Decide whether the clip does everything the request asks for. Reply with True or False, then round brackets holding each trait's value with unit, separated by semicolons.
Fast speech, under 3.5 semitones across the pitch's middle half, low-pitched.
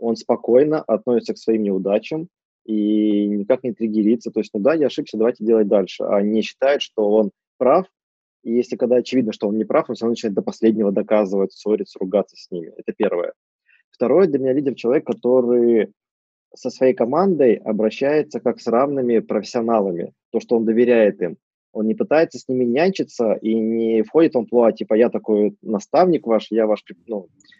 True (180 wpm; 2.9 semitones; 115 Hz)